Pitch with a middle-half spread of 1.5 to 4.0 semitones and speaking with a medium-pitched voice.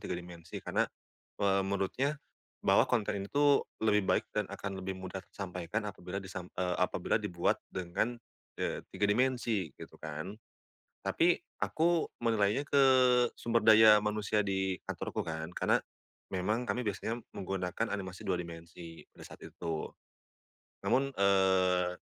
No: average, 3.4 semitones; low, 100 Hz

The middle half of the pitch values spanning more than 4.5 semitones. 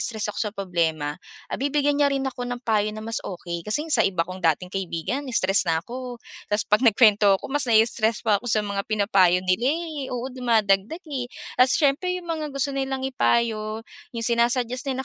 Yes: average, 4.9 semitones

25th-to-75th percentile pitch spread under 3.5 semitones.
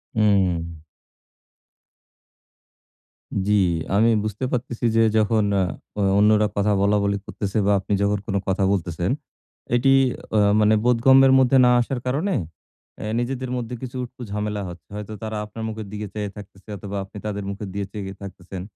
Yes: narrow, 2.6 semitones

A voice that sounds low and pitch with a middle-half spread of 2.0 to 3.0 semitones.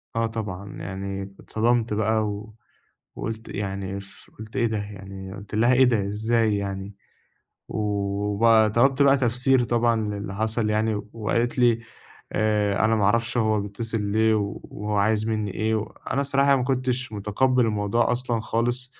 Yes: low, 110 Hz; narrow, 2.5 semitones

